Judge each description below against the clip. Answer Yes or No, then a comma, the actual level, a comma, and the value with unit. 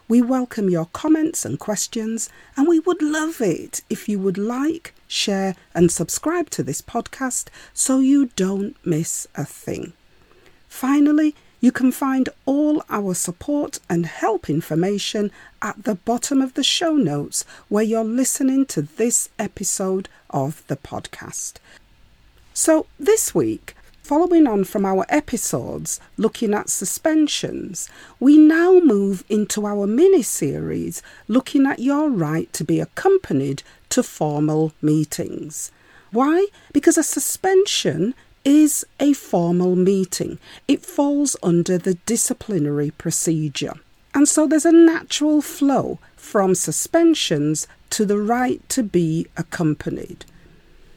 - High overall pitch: Yes, high, 225 Hz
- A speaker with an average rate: No, slow, 130 wpm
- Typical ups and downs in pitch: No, wide, 8.8 semitones